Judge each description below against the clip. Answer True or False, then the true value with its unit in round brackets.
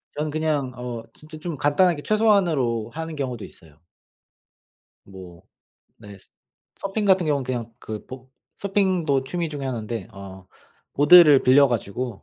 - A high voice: False (140 Hz)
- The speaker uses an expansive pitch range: True (5.8 semitones)